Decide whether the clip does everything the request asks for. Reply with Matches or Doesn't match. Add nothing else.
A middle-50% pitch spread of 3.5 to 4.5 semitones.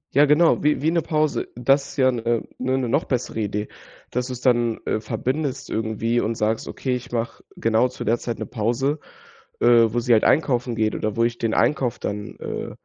Doesn't match